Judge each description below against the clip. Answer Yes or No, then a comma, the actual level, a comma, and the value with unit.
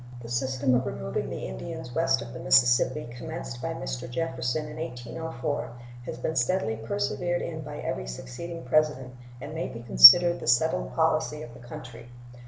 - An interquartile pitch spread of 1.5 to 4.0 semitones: No, average, 4.6 semitones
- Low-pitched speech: Yes, low, 130 Hz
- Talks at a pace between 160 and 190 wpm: Yes, average, 170 wpm